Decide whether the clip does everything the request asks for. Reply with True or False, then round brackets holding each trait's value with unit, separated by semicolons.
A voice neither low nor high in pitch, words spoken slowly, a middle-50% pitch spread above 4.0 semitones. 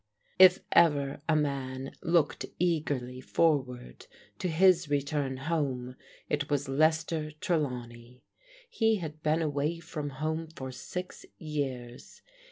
False (150 Hz; 115 wpm; 3.6 semitones)